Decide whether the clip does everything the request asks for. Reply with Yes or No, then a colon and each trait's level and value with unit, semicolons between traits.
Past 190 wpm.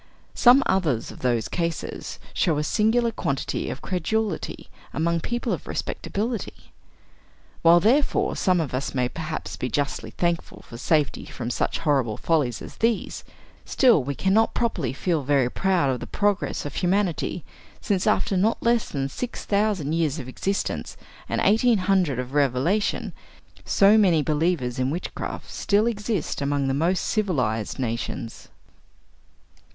No: average, 145 wpm